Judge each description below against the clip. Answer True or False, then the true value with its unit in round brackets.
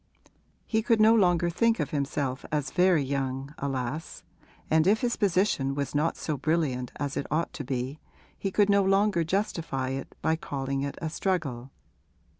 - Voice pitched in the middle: True (155 Hz)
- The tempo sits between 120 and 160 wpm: False (170 wpm)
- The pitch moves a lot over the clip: True (5.7 semitones)